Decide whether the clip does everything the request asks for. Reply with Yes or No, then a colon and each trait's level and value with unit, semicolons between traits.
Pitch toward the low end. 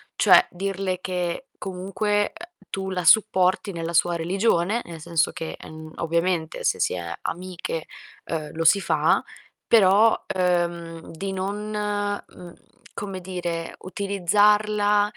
No: medium, 185 Hz